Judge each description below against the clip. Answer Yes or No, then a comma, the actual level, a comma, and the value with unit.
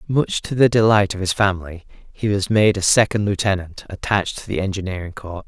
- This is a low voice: Yes, low, 100 Hz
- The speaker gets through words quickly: No, average, 195 wpm